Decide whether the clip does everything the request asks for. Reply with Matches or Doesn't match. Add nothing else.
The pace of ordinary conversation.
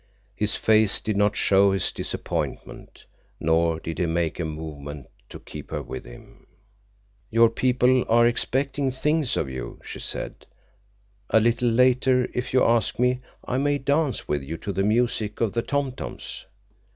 Matches